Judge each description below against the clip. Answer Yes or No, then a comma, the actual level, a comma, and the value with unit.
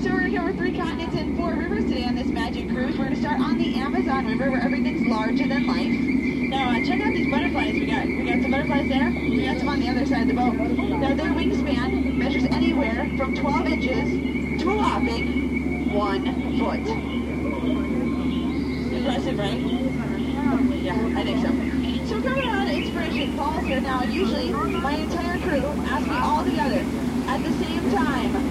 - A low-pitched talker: No, very high, 265 Hz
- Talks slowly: No, average, 185 wpm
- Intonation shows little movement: Yes, narrow, 1.3 semitones